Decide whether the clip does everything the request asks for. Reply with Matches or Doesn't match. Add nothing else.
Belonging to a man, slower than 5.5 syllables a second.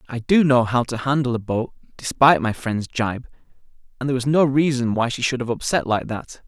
Doesn't match